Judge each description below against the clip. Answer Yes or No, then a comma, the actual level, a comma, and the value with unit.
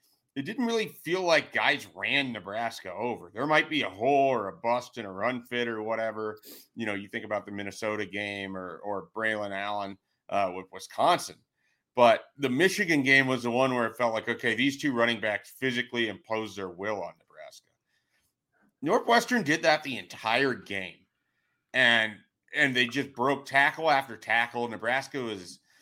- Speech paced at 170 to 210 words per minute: Yes, average, 175 wpm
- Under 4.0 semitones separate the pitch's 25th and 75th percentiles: No, average, 4.5 semitones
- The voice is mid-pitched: No, low, 115 Hz